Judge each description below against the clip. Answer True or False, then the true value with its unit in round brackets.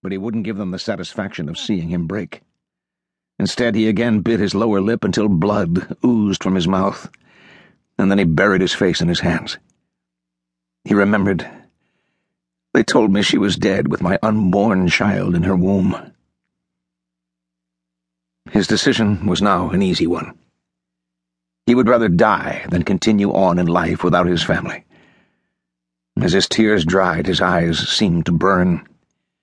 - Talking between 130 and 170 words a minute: True (155 wpm)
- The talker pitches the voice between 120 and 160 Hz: False (85 Hz)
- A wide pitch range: True (8.4 semitones)